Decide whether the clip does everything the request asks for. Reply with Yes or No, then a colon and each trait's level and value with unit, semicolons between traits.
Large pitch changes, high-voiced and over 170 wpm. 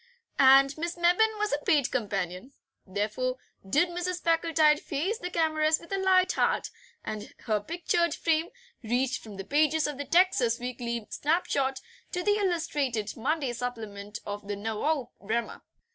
No: wide, 6.7 semitones; very high, 285 Hz; average, 150 wpm